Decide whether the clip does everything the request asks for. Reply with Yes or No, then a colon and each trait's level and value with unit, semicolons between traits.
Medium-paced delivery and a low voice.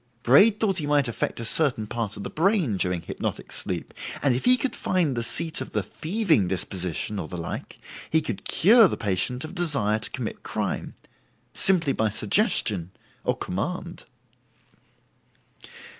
Yes: average, 160 wpm; low, 130 Hz